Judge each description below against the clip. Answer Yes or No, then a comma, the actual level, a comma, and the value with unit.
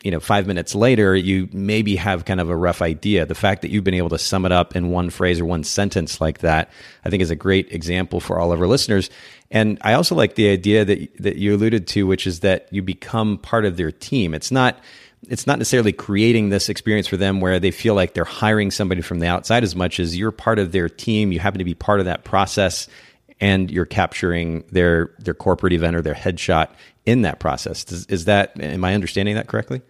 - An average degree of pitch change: Yes, average, 3.0 semitones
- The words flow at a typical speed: No, fast, 240 wpm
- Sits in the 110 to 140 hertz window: No, very low, 95 Hz